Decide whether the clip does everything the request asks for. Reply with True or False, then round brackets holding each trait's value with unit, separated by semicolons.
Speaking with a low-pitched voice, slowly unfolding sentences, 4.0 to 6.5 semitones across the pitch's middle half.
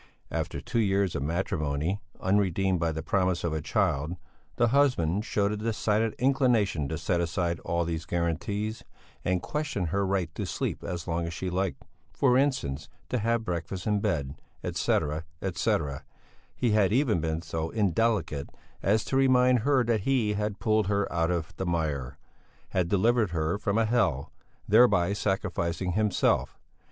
False (95 Hz; 160 wpm; 4.7 semitones)